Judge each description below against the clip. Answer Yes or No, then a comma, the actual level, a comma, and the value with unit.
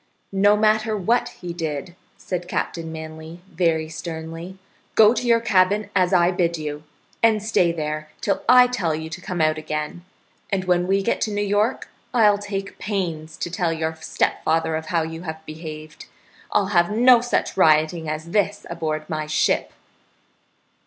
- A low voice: No, medium, 175 Hz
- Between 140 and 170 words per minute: Yes, average, 165 wpm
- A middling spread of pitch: Yes, average, 4.4 semitones